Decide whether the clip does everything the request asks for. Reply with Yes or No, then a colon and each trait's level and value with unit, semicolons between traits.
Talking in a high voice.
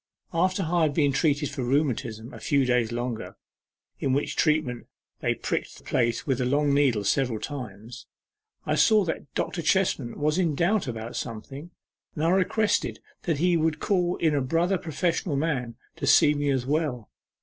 No: medium, 145 Hz